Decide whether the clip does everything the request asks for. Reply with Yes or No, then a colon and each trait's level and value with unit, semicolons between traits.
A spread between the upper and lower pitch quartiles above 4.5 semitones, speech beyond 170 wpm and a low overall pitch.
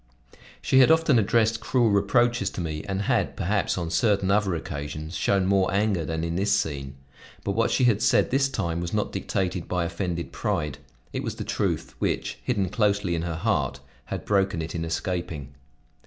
No: average, 4.1 semitones; average, 185 wpm; very low, 95 Hz